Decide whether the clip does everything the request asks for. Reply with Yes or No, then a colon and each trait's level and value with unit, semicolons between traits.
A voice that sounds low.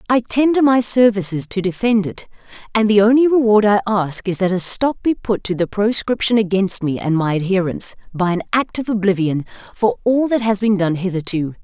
No: high, 205 Hz